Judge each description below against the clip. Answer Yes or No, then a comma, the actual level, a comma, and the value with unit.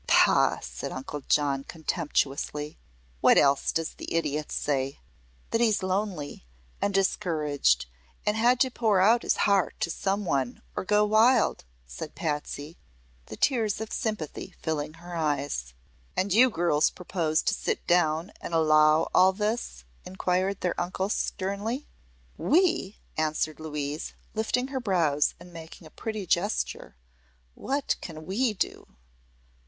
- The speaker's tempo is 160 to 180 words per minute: No, average, 140 wpm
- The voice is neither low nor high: Yes, medium, 175 Hz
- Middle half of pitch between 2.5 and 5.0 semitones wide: No, wide, 5.6 semitones